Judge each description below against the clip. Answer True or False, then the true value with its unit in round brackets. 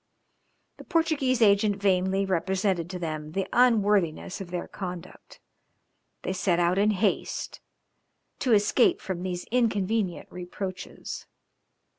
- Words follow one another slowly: True (115 wpm)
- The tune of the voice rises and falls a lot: False (2.8 semitones)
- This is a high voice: True (195 Hz)